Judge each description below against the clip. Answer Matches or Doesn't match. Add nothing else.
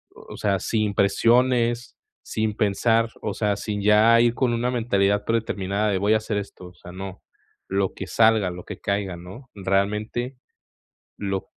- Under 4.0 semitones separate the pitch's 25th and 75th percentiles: Matches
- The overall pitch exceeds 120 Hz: Doesn't match